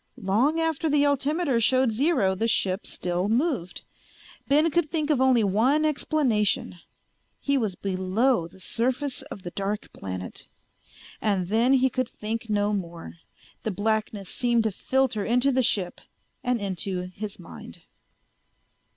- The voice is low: No, high, 230 Hz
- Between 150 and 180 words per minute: No, average, 140 wpm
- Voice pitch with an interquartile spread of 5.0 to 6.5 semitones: Yes, wide, 5.4 semitones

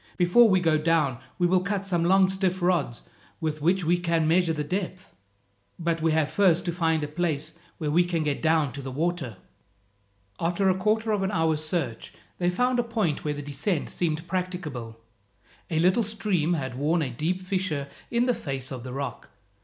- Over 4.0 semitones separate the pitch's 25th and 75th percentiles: No, average, 3.5 semitones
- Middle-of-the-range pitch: Yes, medium, 170 Hz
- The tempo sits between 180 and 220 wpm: Yes, average, 195 wpm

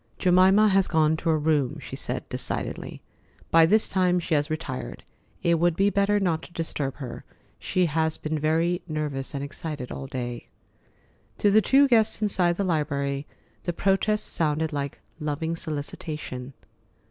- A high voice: No, medium, 160 Hz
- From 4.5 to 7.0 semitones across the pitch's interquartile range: No, average, 4.0 semitones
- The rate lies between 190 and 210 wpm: No, average, 160 wpm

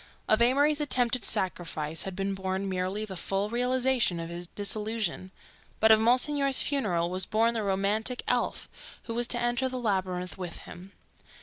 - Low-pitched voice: No, high, 210 Hz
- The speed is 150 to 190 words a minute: Yes, average, 165 wpm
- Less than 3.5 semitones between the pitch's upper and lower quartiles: No, average, 4.4 semitones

